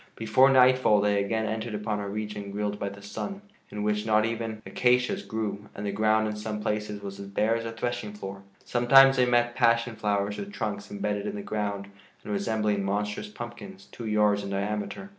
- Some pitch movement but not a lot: No, narrow, 2.3 semitones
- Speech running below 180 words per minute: No, average, 200 wpm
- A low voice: Yes, low, 105 Hz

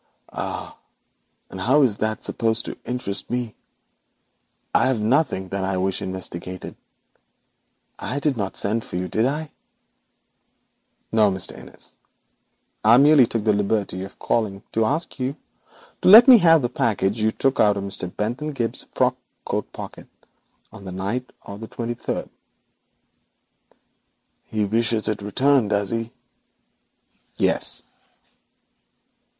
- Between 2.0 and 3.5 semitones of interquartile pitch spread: No, average, 4.3 semitones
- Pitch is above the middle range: No, low, 110 Hz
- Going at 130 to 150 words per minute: Yes, slow, 135 wpm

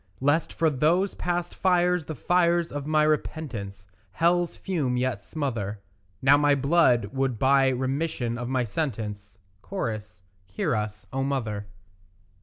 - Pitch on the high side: No, low, 135 Hz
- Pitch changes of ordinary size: No, wide, 5.7 semitones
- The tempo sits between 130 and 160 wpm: Yes, slow, 135 wpm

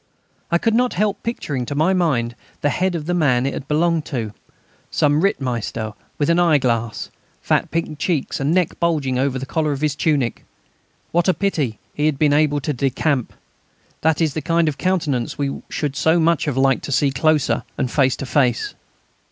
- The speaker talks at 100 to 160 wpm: No, average, 195 wpm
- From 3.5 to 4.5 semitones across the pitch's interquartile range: Yes, average, 3.8 semitones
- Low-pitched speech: No, medium, 150 Hz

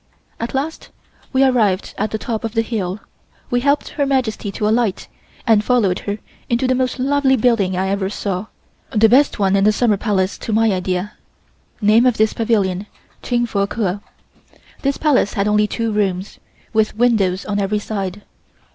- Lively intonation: No, average, 3.5 semitones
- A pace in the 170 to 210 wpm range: Yes, average, 175 wpm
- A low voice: No, high, 215 Hz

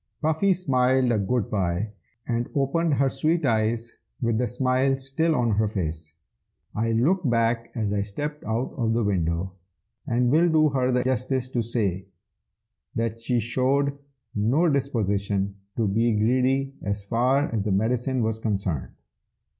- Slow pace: No, average, 155 wpm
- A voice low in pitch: Yes, low, 120 Hz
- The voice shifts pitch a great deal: No, average, 4.0 semitones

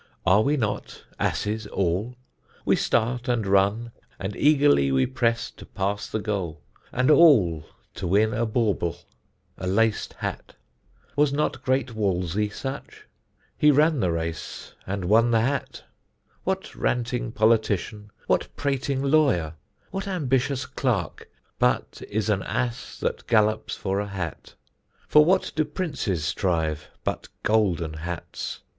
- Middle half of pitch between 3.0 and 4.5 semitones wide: No, wide, 5.4 semitones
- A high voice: No, low, 110 Hz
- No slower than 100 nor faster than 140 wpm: Yes, slow, 135 wpm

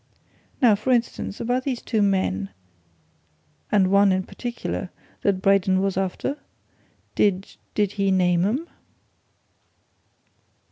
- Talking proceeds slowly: Yes, slow, 110 wpm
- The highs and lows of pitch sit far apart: No, average, 3.4 semitones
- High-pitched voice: Yes, high, 195 Hz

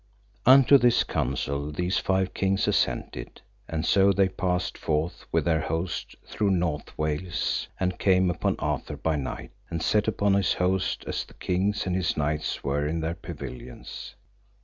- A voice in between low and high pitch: No, very low, 90 Hz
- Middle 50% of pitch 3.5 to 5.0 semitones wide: Yes, average, 3.8 semitones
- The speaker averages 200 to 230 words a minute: No, average, 160 wpm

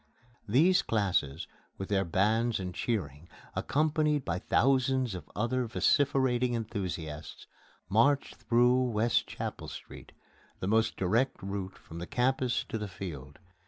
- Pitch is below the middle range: Yes, low, 110 Hz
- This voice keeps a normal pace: No, slow, 125 wpm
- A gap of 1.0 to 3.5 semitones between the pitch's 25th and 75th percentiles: No, wide, 5.4 semitones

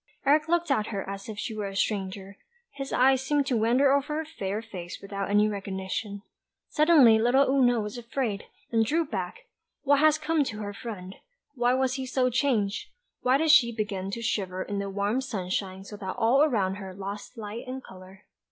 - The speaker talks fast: No, average, 195 wpm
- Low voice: No, high, 225 Hz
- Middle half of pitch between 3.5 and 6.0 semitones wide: Yes, average, 5.1 semitones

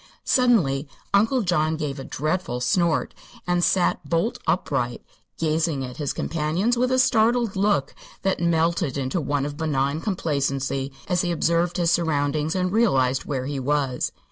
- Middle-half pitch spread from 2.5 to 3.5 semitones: No, average, 4.6 semitones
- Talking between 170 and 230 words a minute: No, average, 150 wpm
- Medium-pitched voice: Yes, medium, 160 Hz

